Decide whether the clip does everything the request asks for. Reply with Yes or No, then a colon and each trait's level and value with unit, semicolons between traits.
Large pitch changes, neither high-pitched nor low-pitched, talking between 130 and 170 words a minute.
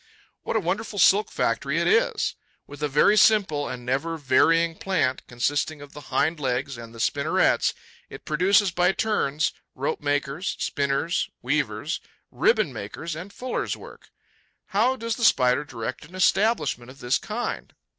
Yes: wide, 6.7 semitones; medium, 160 Hz; average, 155 wpm